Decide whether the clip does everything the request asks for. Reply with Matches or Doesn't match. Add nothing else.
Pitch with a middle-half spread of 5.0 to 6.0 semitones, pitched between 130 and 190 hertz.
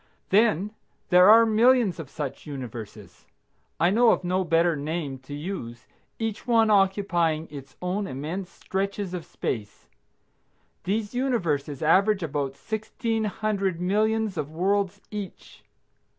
Matches